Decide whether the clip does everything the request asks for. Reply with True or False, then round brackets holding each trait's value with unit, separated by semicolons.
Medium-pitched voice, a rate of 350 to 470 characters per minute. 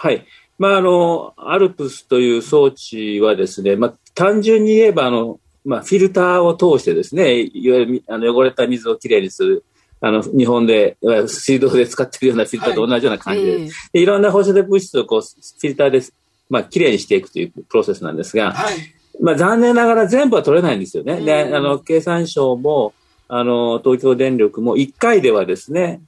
True (160 Hz; 390 characters per minute)